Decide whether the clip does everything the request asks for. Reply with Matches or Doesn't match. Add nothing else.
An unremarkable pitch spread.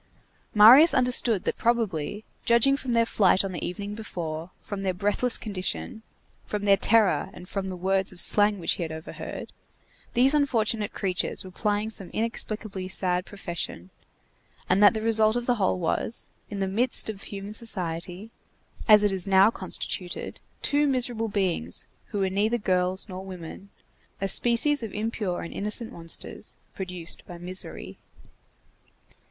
Matches